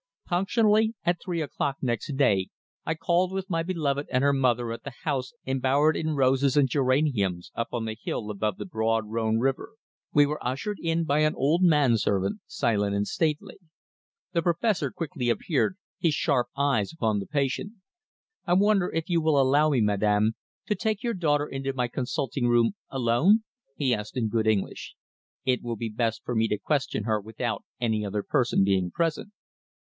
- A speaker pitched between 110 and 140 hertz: Yes, low, 135 Hz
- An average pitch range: No, wide, 6.1 semitones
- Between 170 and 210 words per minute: Yes, average, 180 wpm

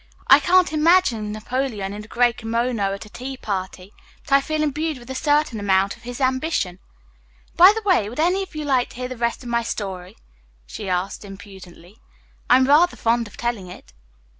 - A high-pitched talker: Yes, high, 240 Hz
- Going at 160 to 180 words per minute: No, average, 195 wpm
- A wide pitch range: Yes, wide, 6.2 semitones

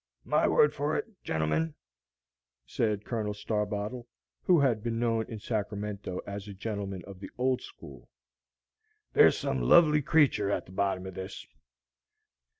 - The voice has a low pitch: Yes, low, 105 Hz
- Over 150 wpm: No, average, 145 wpm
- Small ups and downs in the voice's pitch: No, average, 3.5 semitones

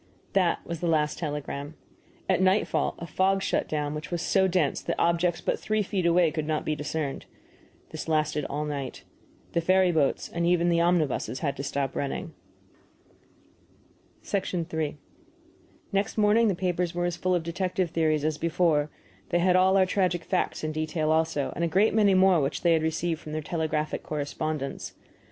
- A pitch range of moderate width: Yes, average, 3.0 semitones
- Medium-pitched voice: Yes, medium, 170 Hz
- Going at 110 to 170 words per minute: No, average, 180 wpm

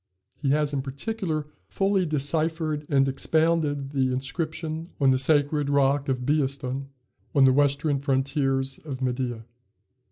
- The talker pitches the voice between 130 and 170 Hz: Yes, medium, 140 Hz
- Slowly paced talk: Yes, slow, 130 wpm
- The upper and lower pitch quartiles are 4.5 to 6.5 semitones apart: No, narrow, 2.5 semitones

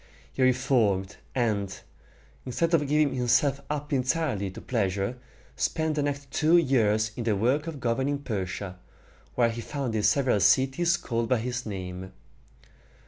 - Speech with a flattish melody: No, average, 5.2 semitones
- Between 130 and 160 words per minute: Yes, average, 140 wpm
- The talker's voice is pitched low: Yes, low, 125 Hz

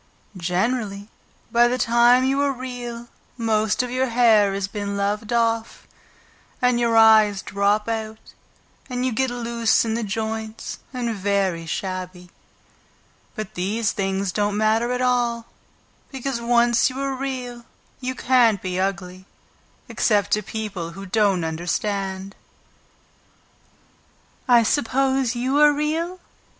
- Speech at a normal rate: No, slow, 130 wpm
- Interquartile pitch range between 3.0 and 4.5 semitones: Yes, average, 3.6 semitones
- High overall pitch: Yes, high, 225 Hz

